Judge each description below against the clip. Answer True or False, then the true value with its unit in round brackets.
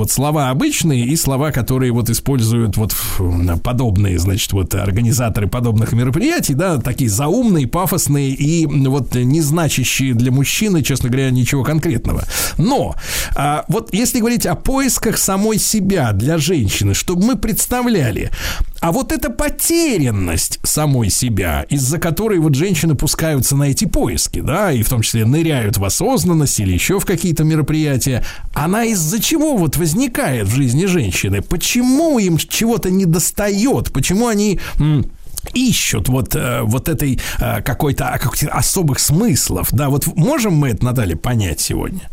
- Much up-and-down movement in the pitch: True (6.8 semitones)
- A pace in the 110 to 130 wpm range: False (145 wpm)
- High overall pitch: False (140 Hz)